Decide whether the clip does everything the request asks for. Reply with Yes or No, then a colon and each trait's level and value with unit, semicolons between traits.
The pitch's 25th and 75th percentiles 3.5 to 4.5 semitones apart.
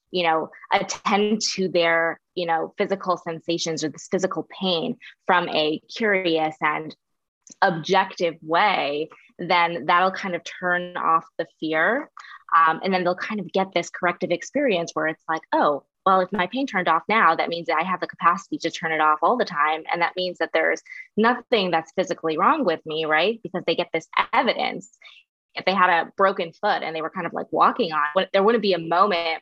No: average, 2.8 semitones